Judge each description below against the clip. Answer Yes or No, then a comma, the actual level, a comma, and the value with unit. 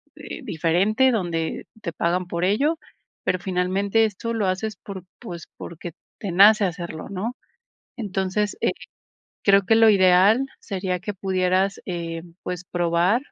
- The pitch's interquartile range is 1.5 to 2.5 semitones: No, average, 2.9 semitones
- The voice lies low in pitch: No, high, 190 Hz